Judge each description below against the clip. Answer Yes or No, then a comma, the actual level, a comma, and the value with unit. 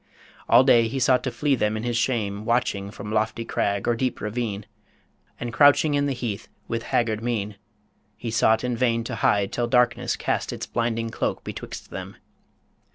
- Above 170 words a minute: Yes, average, 180 wpm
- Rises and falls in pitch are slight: Yes, narrow, 2.3 semitones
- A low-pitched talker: Yes, low, 115 Hz